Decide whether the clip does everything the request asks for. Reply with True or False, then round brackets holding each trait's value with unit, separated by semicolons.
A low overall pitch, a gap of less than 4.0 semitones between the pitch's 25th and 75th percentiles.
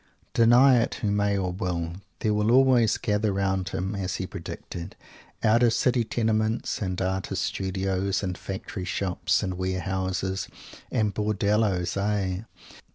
True (100 Hz; 2.6 semitones)